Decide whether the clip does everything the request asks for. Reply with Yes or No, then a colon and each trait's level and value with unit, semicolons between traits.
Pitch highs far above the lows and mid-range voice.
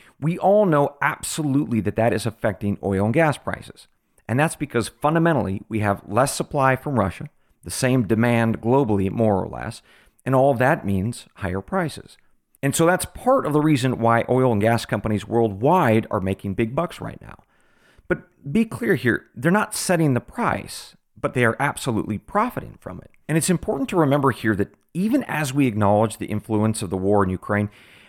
No: wide, 6.0 semitones; low, 120 Hz